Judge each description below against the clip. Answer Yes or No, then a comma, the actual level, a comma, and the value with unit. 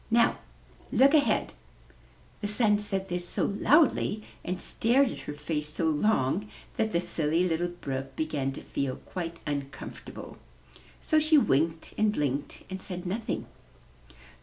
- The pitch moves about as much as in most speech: No, wide, 6.1 semitones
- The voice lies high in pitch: No, medium, 180 Hz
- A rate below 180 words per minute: Yes, average, 140 wpm